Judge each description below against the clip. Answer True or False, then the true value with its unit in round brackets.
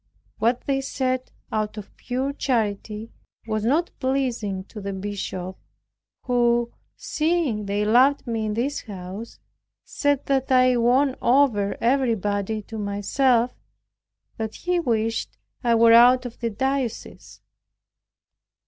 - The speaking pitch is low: False (235 Hz)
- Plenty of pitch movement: False (3.7 semitones)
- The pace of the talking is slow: True (125 wpm)